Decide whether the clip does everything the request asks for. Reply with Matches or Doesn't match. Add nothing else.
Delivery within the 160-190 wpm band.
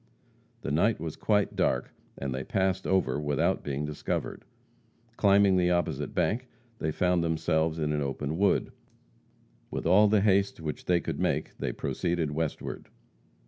Doesn't match